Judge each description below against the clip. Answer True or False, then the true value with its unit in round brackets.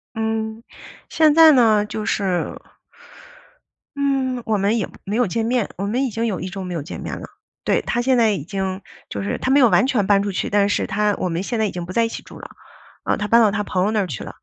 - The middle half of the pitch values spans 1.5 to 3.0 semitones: False (3.4 semitones)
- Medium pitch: False (210 Hz)